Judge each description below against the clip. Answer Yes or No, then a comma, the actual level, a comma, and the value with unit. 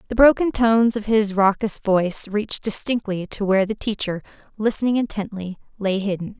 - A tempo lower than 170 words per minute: Yes, average, 160 wpm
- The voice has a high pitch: Yes, high, 210 Hz